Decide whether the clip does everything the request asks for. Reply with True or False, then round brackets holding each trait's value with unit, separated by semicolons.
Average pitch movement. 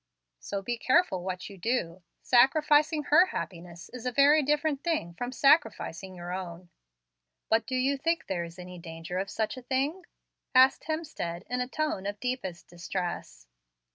False (7.9 semitones)